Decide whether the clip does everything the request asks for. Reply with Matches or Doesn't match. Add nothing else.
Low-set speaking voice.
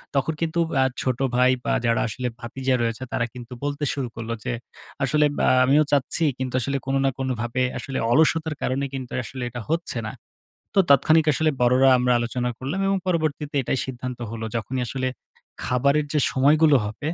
Matches